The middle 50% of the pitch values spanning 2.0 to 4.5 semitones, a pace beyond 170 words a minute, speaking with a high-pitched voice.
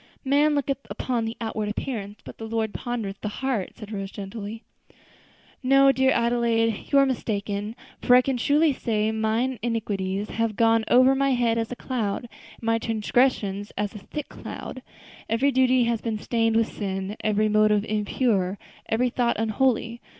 No: average, 2.9 semitones; average, 165 wpm; high, 225 Hz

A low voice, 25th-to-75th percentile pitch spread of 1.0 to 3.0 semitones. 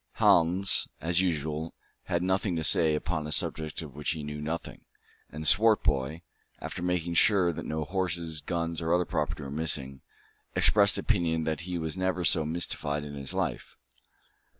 Yes: very low, 80 Hz; narrow, 2.6 semitones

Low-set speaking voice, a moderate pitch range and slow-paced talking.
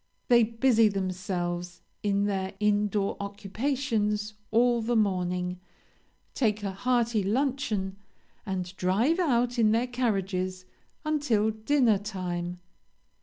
No: high, 210 Hz; average, 3.8 semitones; slow, 110 wpm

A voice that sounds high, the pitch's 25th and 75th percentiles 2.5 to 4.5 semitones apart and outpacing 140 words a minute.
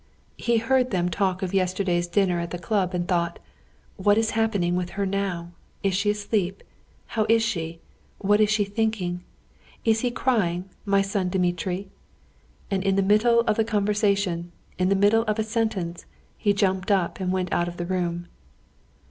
Yes: high, 195 Hz; average, 3.1 semitones; average, 180 wpm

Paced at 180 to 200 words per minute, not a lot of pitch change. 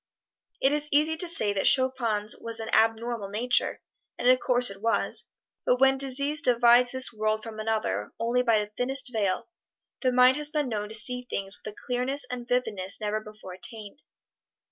No: average, 185 wpm; average, 3.2 semitones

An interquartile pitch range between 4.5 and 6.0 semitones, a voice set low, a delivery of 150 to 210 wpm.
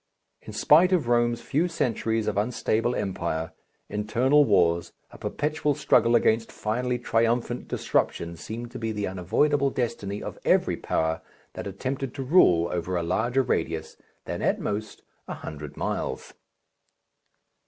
No: average, 4.8 semitones; low, 115 Hz; average, 140 wpm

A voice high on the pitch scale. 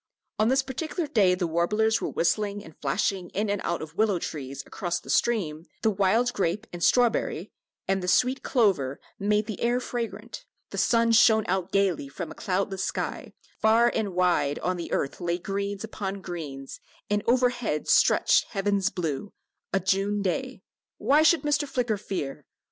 Yes: high, 200 Hz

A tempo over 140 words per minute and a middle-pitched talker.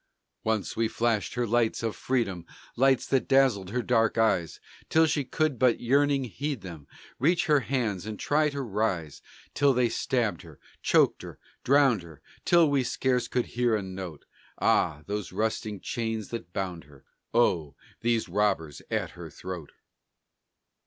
No: average, 160 wpm; low, 115 Hz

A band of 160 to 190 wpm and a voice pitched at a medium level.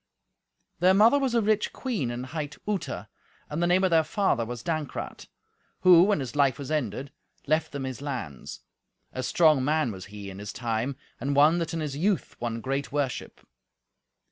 Yes: average, 185 wpm; medium, 145 Hz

